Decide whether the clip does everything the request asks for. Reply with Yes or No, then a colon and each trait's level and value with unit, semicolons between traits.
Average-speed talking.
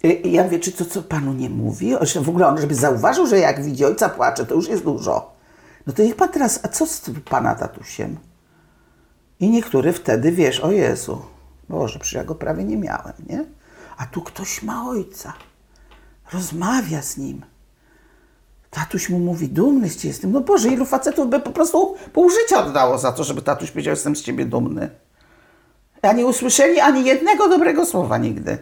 No: fast, 190 wpm